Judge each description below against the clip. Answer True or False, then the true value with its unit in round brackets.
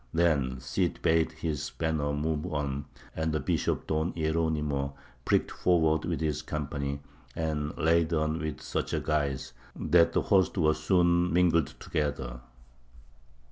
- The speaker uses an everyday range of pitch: False (2.2 semitones)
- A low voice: True (80 Hz)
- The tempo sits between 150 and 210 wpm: False (140 wpm)